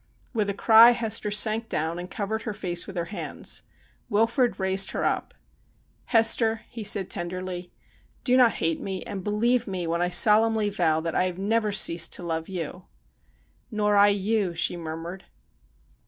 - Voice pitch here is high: Yes, high, 200 Hz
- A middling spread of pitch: Yes, average, 3.8 semitones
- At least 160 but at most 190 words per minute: Yes, average, 180 wpm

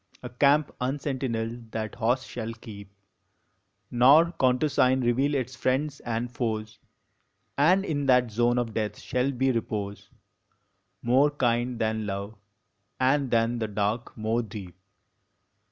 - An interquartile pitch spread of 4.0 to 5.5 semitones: No, average, 3.0 semitones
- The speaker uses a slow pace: Yes, slow, 125 wpm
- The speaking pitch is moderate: No, low, 120 Hz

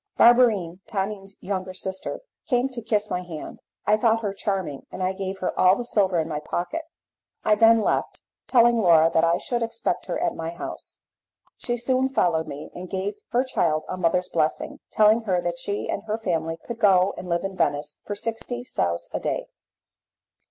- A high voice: Yes, high, 195 Hz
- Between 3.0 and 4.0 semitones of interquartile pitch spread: No, average, 4.7 semitones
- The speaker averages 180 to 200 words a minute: Yes, average, 190 wpm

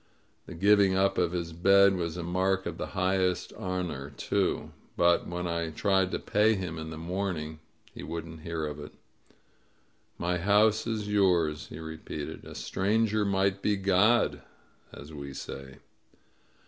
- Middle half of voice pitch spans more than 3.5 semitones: No, average, 3.2 semitones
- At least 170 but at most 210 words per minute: No, average, 155 wpm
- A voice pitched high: No, very low, 90 Hz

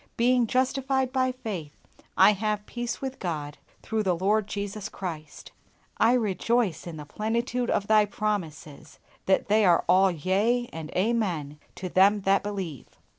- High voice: Yes, high, 205 Hz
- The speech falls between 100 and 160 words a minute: Yes, average, 150 wpm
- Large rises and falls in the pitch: No, average, 4.5 semitones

